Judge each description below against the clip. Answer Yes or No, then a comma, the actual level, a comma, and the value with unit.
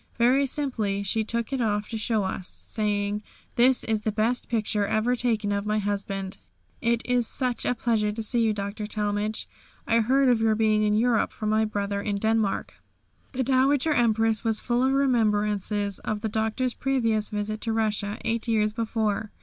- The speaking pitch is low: No, high, 220 Hz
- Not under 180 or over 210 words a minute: Yes, average, 185 wpm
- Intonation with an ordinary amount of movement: No, narrow, 2.2 semitones